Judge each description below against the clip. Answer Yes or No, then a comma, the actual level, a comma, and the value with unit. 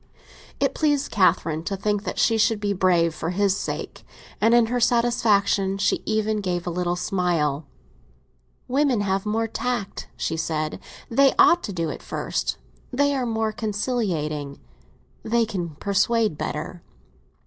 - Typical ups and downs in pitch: Yes, average, 4.5 semitones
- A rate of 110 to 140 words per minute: No, average, 150 wpm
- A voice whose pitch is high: Yes, high, 205 Hz